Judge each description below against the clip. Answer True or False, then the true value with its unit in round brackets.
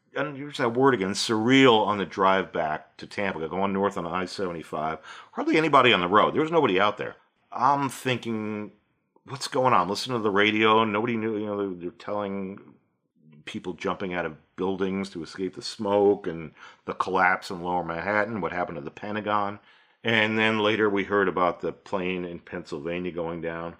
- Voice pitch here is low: True (100 Hz)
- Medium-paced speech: True (185 wpm)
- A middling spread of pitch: True (3.1 semitones)